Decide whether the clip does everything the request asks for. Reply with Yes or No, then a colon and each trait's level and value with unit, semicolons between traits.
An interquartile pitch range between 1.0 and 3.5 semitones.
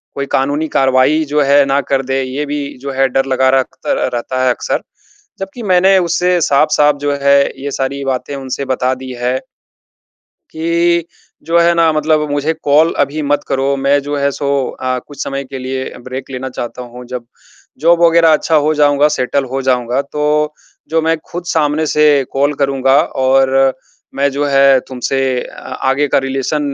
Yes: narrow, 2.4 semitones